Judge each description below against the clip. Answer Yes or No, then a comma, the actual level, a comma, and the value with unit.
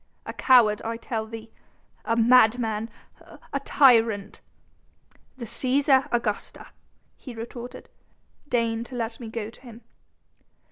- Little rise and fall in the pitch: Yes, narrow, 1.9 semitones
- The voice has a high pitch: Yes, high, 230 Hz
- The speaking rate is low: Yes, slow, 125 wpm